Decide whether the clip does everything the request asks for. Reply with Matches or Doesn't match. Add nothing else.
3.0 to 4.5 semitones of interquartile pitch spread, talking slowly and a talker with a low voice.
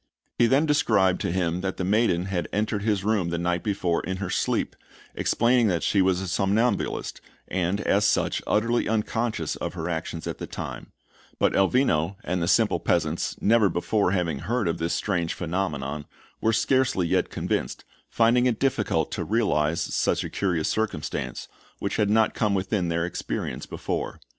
Doesn't match